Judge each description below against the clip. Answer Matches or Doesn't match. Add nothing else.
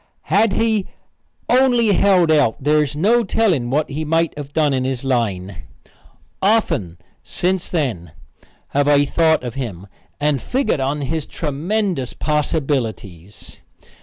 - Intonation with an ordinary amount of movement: Doesn't match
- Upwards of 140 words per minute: Doesn't match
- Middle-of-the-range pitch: Matches